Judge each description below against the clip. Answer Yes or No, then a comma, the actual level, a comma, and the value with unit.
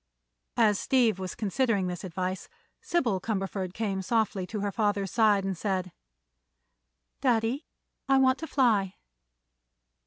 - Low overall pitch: No, high, 205 Hz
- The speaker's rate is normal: No, slow, 125 wpm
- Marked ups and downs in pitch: No, average, 3.5 semitones